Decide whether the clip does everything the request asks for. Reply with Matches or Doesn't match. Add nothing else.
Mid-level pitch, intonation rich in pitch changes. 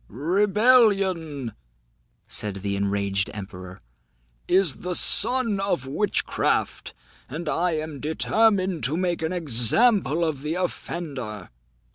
Matches